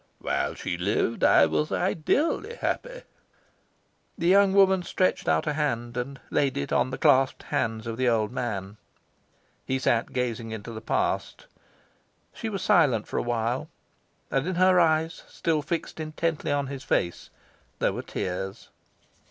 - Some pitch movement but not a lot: No, wide, 6.7 semitones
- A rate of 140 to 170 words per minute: Yes, average, 155 wpm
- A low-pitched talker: Yes, low, 130 Hz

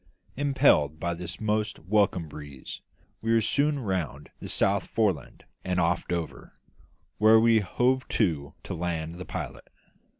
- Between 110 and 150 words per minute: Yes, average, 140 wpm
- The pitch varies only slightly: No, average, 5.1 semitones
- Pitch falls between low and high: No, very low, 95 Hz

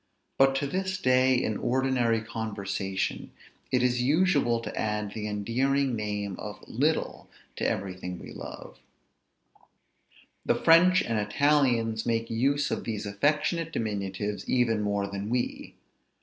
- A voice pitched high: No, low, 115 Hz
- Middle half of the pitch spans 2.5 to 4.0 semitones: No, average, 4.6 semitones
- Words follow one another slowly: Yes, slow, 130 wpm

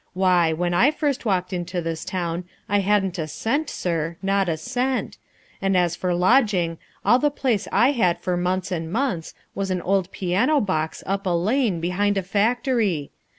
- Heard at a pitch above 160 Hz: Yes, medium, 185 Hz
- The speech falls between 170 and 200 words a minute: Yes, average, 180 wpm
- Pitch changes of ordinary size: Yes, average, 3.6 semitones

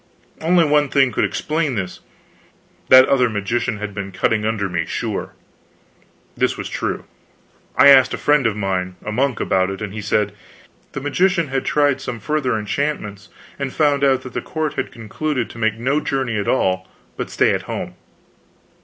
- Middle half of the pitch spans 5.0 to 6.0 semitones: Yes, average, 5.3 semitones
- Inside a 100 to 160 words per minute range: No, average, 180 wpm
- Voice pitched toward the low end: Yes, low, 125 Hz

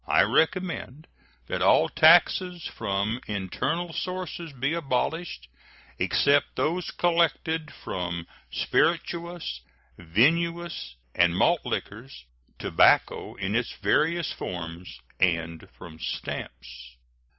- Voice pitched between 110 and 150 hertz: Yes, low, 135 Hz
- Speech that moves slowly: Yes, slow, 95 wpm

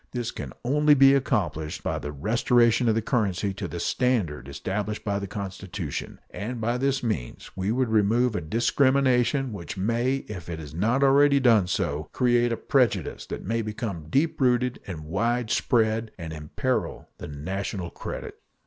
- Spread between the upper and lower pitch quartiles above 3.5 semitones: Yes, average, 5.0 semitones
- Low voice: Yes, low, 110 Hz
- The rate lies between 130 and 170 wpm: Yes, average, 165 wpm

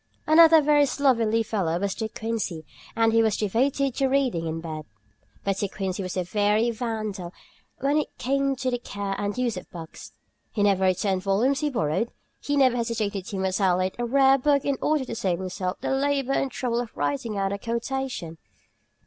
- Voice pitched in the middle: No, high, 225 Hz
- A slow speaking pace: No, average, 190 wpm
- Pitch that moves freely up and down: Yes, wide, 5.8 semitones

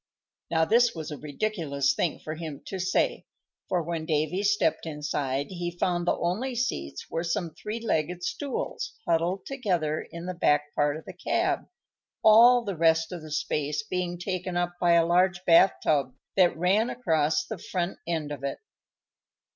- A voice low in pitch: No, medium, 175 Hz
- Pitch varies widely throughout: No, average, 3.4 semitones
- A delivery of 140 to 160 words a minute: No, average, 170 wpm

